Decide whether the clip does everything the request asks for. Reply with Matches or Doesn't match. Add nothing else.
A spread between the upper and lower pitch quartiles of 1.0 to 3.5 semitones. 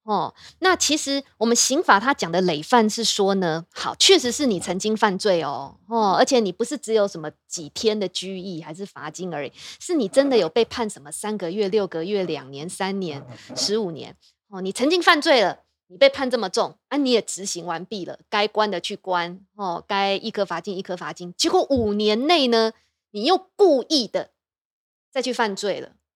Doesn't match